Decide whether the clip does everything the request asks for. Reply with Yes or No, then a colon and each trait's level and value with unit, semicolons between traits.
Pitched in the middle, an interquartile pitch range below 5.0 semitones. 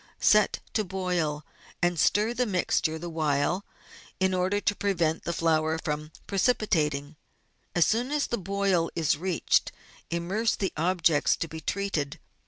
Yes: medium, 175 Hz; average, 4.0 semitones